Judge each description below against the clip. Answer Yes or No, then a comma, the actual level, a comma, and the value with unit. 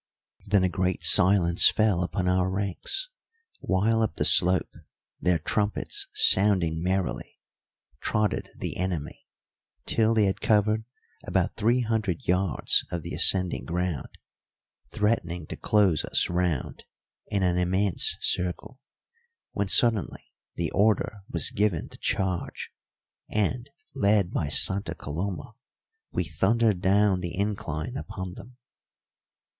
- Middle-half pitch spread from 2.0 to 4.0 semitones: Yes, average, 3.1 semitones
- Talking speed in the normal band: No, slow, 120 wpm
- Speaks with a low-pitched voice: Yes, very low, 95 Hz